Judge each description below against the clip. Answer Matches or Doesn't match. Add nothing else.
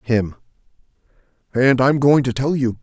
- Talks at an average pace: Matches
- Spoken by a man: Matches